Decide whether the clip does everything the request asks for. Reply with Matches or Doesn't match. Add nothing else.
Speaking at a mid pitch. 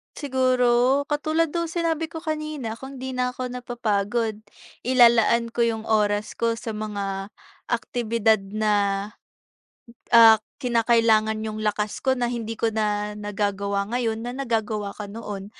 Doesn't match